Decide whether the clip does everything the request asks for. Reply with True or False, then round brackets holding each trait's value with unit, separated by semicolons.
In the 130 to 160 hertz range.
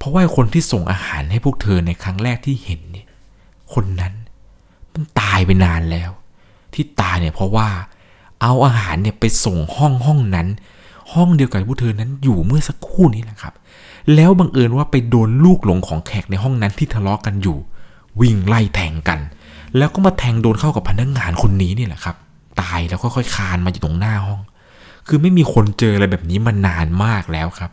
False (105 Hz)